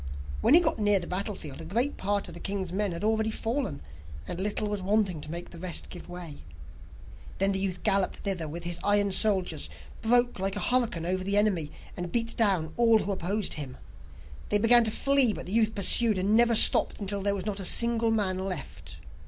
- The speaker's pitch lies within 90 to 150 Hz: No, high, 200 Hz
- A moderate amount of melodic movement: Yes, average, 3.5 semitones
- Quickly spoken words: Yes, fast, 210 wpm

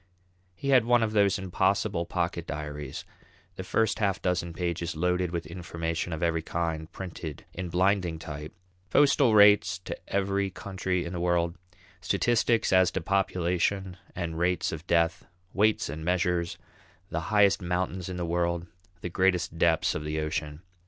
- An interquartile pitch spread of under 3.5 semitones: Yes, narrow, 2.6 semitones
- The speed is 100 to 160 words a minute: Yes, average, 155 wpm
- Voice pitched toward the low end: Yes, very low, 90 Hz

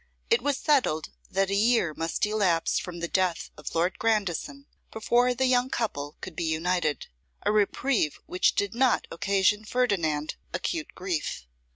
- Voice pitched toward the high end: Yes, high, 200 Hz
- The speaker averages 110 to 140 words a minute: No, average, 155 wpm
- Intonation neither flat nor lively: No, wide, 6.1 semitones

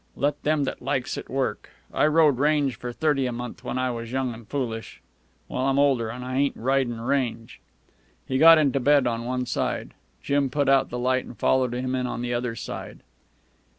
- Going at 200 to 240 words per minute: Yes, fast, 205 wpm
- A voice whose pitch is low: Yes, low, 130 Hz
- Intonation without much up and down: Yes, narrow, 2.3 semitones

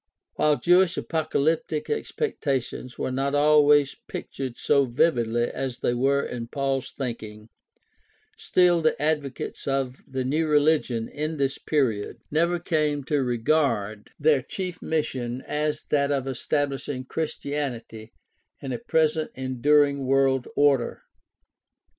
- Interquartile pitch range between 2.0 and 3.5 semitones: Yes, average, 3.0 semitones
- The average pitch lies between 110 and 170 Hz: Yes, medium, 140 Hz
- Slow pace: Yes, slow, 120 wpm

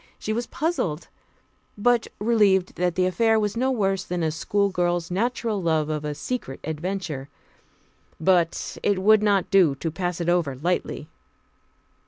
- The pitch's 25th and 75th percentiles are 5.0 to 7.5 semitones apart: No, average, 4.3 semitones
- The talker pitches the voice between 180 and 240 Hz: Yes, medium, 185 Hz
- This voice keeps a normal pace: Yes, average, 150 wpm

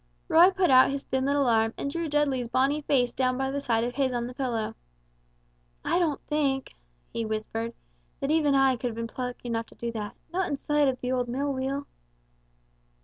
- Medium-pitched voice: No, very high, 260 Hz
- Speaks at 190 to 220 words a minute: Yes, fast, 205 wpm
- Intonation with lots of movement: No, average, 2.9 semitones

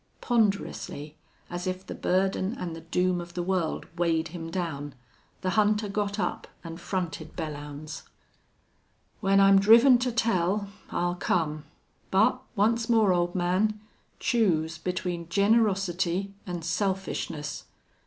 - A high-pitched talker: No, medium, 180 Hz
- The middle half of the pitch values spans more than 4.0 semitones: No, average, 3.3 semitones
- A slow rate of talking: Yes, slow, 125 wpm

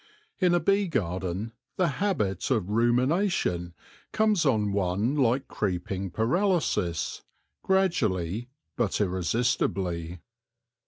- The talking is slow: Yes, slow, 95 wpm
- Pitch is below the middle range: Yes, low, 110 Hz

